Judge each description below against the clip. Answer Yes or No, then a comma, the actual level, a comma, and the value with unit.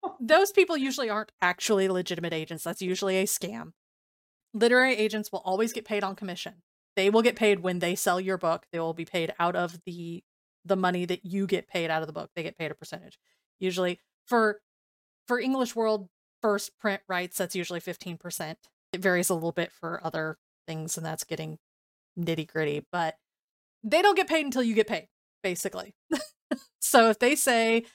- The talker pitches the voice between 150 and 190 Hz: Yes, medium, 185 Hz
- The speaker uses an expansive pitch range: No, average, 4.6 semitones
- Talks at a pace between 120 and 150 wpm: No, average, 185 wpm